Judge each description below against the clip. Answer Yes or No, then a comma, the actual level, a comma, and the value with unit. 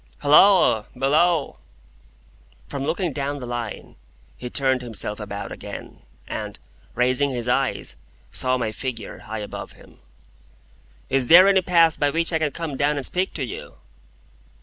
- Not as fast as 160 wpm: Yes, average, 150 wpm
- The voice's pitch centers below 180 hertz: Yes, medium, 140 Hz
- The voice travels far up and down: No, average, 4.7 semitones